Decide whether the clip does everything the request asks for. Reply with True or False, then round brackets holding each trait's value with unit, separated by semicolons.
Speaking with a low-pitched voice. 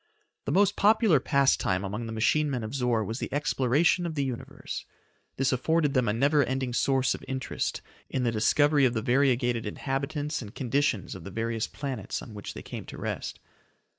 True (130 Hz)